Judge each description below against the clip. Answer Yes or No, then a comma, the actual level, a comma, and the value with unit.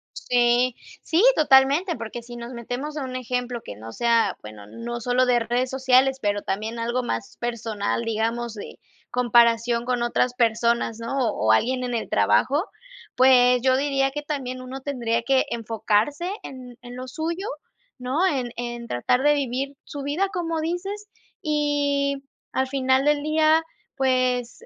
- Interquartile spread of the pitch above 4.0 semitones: No, average, 2.8 semitones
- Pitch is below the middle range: No, very high, 250 Hz